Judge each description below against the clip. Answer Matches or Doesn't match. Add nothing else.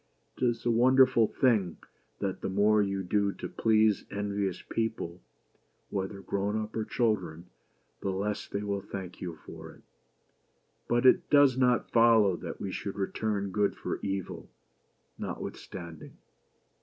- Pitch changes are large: Doesn't match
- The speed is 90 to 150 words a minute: Matches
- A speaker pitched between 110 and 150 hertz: Doesn't match